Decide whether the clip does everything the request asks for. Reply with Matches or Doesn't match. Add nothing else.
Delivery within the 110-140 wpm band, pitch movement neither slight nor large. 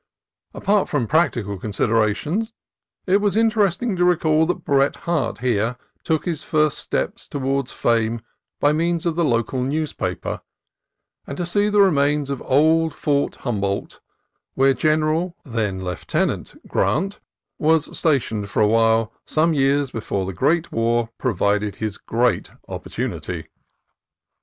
Doesn't match